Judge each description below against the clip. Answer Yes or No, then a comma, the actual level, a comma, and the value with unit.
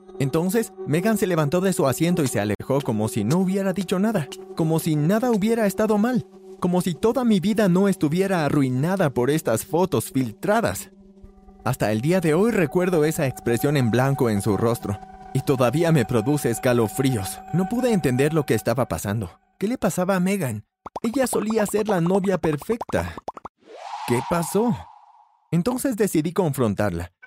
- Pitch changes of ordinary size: No, wide, 7.0 semitones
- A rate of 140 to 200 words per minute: Yes, average, 165 wpm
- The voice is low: No, medium, 175 Hz